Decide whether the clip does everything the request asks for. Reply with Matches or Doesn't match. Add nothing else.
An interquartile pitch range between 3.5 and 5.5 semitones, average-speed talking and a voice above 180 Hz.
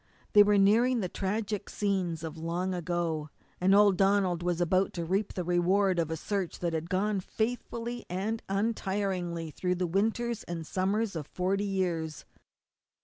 Doesn't match